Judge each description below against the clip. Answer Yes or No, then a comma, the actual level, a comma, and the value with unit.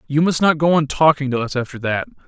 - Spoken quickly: Yes, fast, 265 wpm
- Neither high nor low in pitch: Yes, medium, 145 Hz